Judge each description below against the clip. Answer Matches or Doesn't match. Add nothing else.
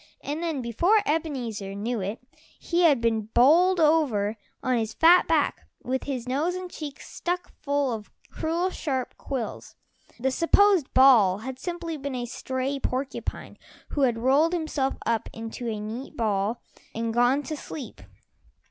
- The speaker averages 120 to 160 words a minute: Matches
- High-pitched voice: Matches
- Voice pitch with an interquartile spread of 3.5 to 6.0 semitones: Matches